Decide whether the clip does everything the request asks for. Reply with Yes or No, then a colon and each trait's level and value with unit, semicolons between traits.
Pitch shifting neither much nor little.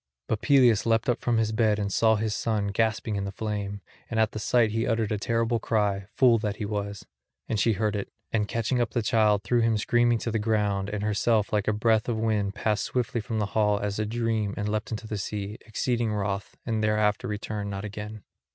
No: narrow, 1.6 semitones